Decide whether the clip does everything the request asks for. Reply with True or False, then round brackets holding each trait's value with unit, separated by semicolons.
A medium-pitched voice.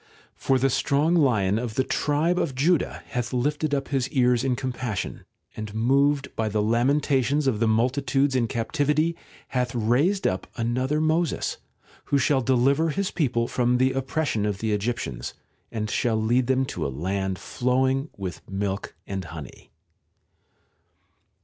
False (125 Hz)